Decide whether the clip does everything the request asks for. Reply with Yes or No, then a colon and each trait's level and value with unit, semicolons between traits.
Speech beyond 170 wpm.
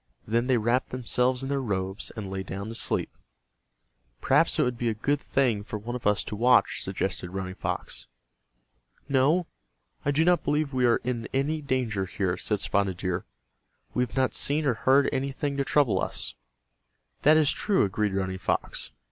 Yes: average, 180 wpm